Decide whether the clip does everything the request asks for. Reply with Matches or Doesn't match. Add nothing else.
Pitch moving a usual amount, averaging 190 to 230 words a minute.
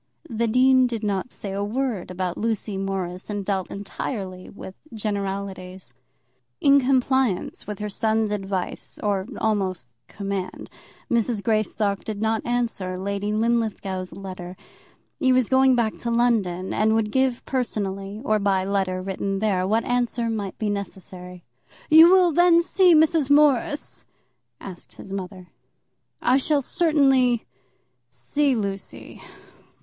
Doesn't match